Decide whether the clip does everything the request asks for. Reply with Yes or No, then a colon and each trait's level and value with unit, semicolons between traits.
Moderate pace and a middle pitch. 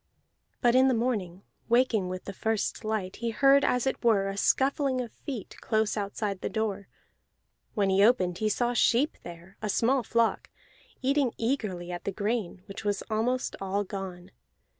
No: average, 170 wpm; high, 215 Hz